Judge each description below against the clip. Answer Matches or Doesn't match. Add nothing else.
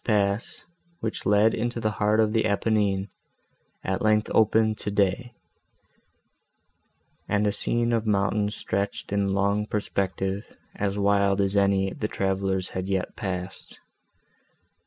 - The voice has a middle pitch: Doesn't match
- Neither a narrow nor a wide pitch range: Doesn't match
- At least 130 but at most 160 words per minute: Matches